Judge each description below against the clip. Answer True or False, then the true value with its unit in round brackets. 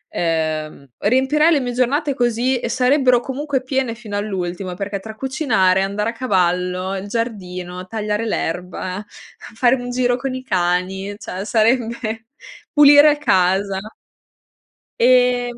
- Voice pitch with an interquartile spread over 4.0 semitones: True (5.3 semitones)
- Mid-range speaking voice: False (225 Hz)